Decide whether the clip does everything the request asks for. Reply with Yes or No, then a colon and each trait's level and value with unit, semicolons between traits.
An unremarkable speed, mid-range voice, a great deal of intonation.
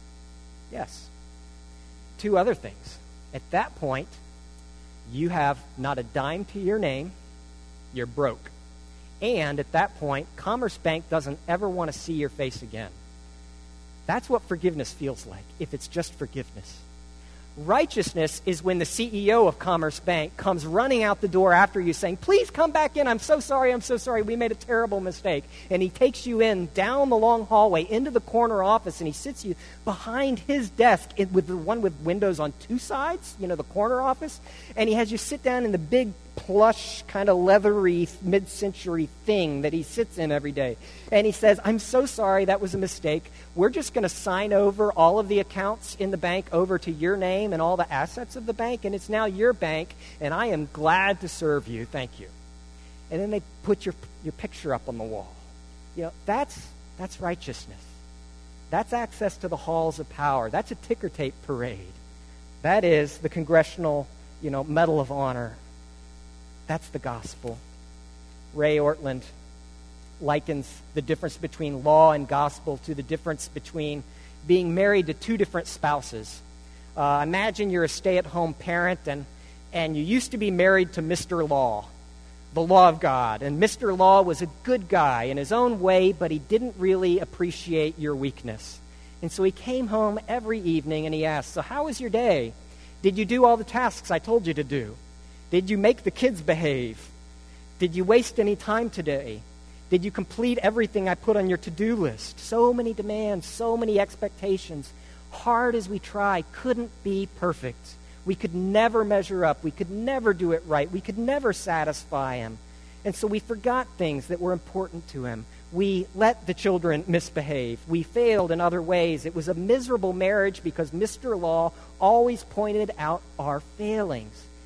Yes: average, 185 wpm; medium, 175 Hz; wide, 7.1 semitones